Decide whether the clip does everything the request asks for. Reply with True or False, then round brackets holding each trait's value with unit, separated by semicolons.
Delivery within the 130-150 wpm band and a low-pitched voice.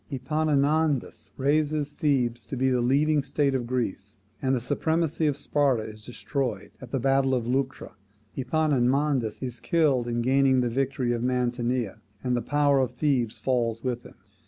False (160 wpm; 130 Hz)